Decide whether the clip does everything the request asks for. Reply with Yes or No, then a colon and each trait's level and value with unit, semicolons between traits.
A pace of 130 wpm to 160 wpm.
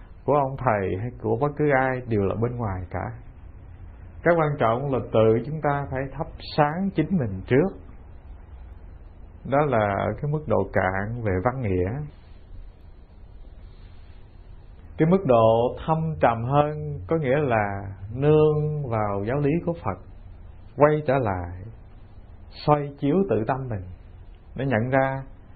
Yes: average, 145 wpm